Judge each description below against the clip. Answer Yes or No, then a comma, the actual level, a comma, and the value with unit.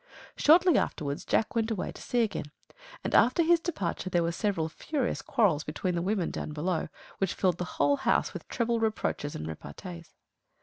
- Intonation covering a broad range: Yes, wide, 5.9 semitones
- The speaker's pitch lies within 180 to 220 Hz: Yes, high, 190 Hz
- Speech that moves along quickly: No, average, 180 wpm